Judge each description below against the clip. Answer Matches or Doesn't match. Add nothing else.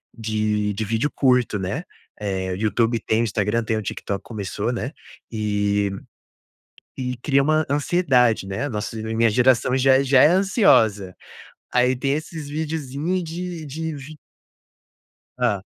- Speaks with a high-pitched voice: Doesn't match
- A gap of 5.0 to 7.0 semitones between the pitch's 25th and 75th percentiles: Matches